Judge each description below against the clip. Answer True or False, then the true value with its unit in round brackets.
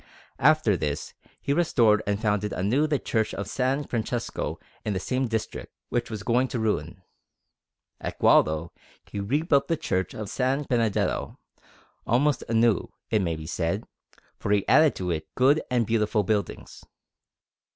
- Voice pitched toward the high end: False (110 Hz)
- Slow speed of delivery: False (150 wpm)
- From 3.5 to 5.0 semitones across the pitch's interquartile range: True (4.5 semitones)